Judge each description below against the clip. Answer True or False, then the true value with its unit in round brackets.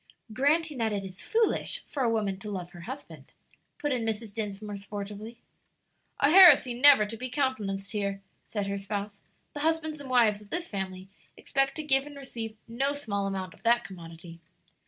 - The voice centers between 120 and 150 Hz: False (220 Hz)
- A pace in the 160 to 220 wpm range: True (180 wpm)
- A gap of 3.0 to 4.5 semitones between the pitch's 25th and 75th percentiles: False (5.5 semitones)